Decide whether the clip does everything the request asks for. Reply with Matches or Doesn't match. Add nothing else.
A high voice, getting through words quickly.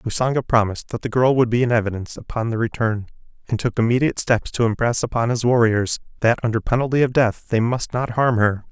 Doesn't match